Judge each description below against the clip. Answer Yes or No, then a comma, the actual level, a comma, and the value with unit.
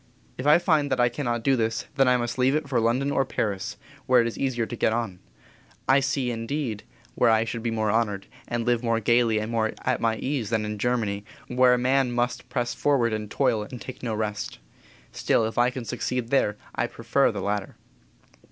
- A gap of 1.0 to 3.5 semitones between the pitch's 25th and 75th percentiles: Yes, narrow, 2.4 semitones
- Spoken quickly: Yes, fast, 215 wpm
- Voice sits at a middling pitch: No, low, 120 Hz